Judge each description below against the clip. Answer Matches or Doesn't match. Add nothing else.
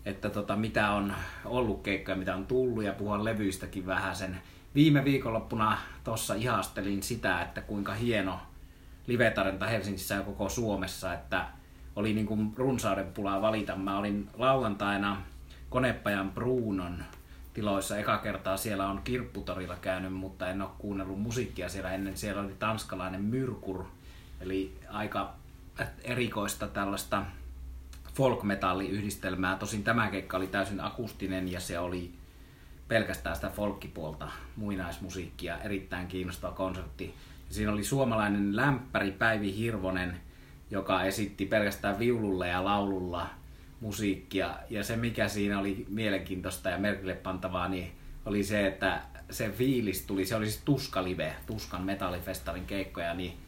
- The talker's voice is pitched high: Doesn't match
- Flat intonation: Matches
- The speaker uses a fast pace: Doesn't match